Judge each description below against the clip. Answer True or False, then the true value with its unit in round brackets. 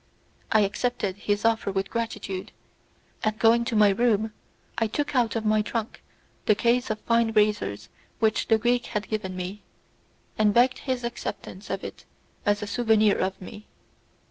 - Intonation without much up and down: True (2.2 semitones)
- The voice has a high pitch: True (215 Hz)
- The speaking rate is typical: True (170 wpm)